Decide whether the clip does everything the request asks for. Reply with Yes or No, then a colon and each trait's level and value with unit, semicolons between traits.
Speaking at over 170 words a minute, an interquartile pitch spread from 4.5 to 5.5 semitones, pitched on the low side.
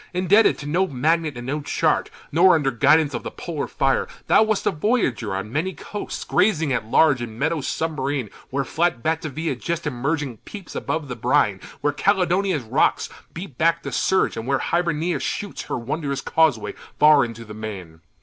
No: average, 180 wpm; average, 5.2 semitones; medium, 150 Hz